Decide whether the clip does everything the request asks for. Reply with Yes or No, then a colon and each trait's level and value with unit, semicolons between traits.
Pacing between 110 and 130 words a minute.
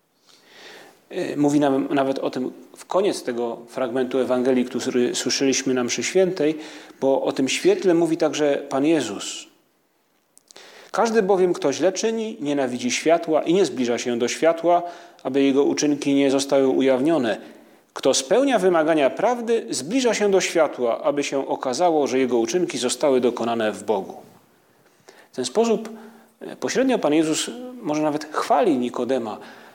No: average, 140 wpm